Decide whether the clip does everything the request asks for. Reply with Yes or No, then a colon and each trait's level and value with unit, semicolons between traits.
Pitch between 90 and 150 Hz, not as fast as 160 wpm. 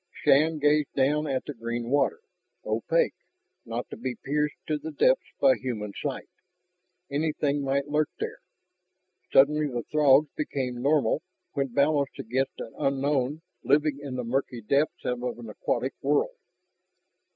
Yes: medium, 140 Hz; average, 140 wpm